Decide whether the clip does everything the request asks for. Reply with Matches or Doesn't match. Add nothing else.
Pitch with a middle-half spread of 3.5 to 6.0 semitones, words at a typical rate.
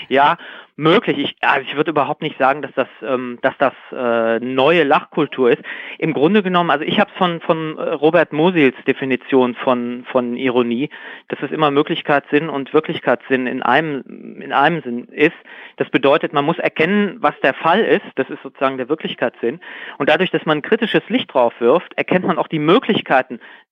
Matches